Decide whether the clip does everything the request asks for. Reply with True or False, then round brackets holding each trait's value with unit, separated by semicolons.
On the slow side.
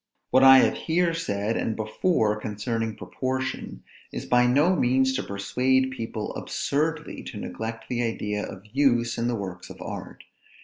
False (160 wpm)